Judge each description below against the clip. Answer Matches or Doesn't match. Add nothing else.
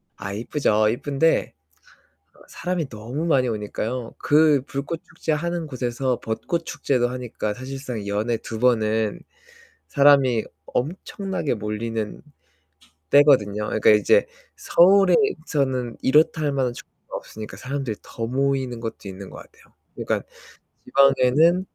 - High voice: Doesn't match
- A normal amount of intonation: Matches